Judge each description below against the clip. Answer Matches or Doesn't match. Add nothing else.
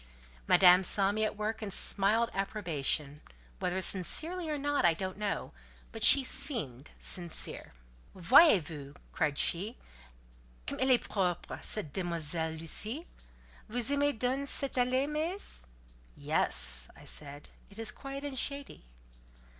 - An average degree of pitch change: Doesn't match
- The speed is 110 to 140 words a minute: Matches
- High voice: Matches